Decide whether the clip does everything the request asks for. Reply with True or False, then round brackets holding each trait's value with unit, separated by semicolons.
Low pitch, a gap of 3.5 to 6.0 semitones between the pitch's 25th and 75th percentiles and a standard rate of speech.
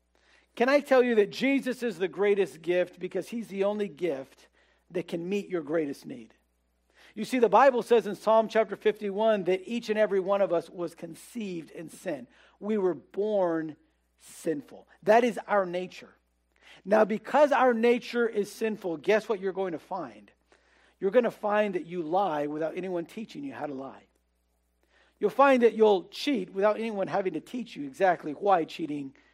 False (200 Hz; 4.3 semitones; 180 wpm)